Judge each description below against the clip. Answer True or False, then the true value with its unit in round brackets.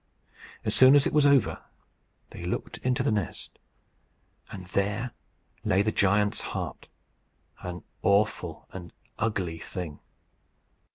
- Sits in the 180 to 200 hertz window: False (100 Hz)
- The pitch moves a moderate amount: True (4.9 semitones)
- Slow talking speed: True (120 wpm)